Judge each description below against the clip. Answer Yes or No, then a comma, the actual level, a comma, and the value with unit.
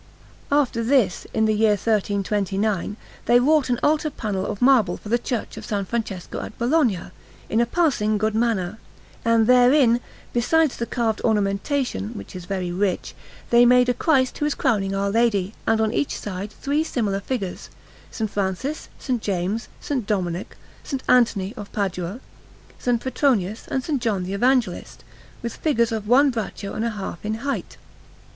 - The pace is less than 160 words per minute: No, average, 165 wpm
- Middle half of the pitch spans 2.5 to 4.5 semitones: Yes, average, 3.9 semitones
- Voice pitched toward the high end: Yes, high, 220 Hz